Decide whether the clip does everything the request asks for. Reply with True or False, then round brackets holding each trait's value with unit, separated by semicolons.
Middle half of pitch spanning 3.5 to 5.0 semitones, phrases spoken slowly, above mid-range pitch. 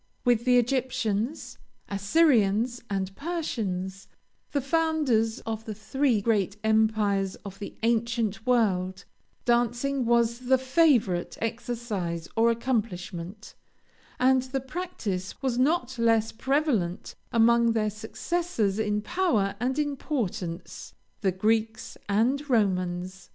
True (4.4 semitones; 110 wpm; 225 Hz)